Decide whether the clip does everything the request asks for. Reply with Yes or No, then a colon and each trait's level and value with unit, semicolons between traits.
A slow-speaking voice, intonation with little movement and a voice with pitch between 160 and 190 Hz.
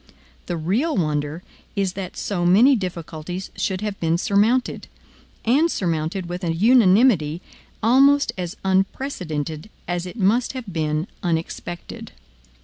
No: slow, 125 wpm; average, 4.9 semitones; medium, 185 Hz